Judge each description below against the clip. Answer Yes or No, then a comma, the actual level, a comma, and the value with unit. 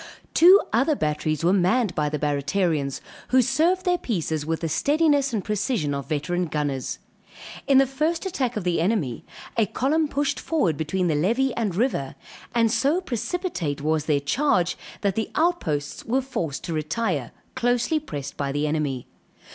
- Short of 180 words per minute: Yes, average, 165 wpm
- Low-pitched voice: No, medium, 185 Hz